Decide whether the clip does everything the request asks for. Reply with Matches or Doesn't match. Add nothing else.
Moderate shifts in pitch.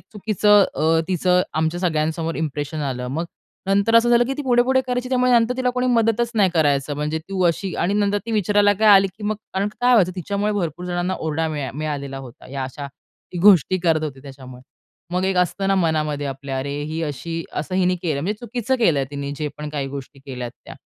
Doesn't match